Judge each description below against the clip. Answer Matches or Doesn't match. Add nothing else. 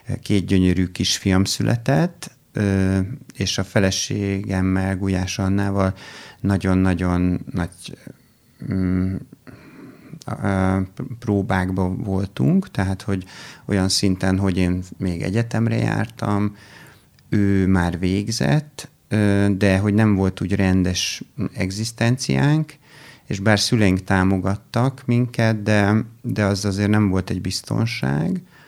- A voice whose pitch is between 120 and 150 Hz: Doesn't match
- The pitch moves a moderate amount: Matches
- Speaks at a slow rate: Matches